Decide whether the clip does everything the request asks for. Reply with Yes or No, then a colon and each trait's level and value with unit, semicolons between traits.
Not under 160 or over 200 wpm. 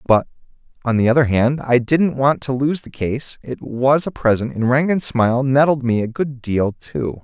Yes: average, 190 wpm